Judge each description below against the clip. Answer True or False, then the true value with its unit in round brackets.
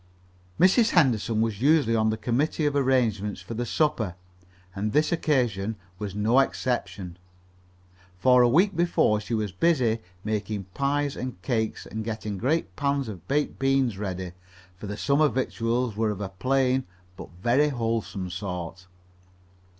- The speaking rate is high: False (150 wpm)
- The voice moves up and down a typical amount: True (4.7 semitones)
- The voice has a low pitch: True (115 Hz)